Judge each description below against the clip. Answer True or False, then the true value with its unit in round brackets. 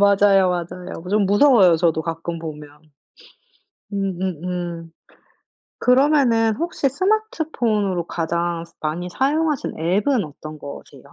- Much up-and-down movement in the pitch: True (6.4 semitones)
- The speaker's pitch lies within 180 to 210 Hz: True (185 Hz)